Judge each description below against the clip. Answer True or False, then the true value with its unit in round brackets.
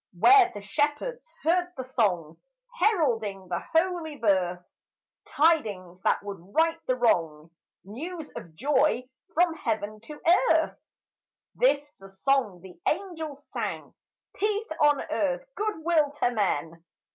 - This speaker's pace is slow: True (125 wpm)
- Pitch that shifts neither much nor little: False (9.0 semitones)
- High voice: True (275 Hz)